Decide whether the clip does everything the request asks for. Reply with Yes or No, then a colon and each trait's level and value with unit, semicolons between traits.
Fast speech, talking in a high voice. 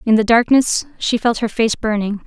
Yes: fast, 210 wpm; high, 225 Hz